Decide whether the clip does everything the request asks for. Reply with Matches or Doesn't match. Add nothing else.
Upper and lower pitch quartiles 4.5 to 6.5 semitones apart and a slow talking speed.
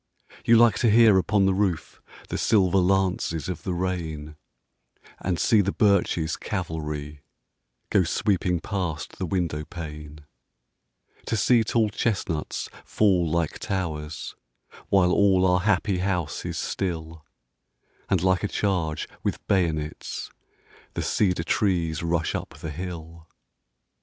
Doesn't match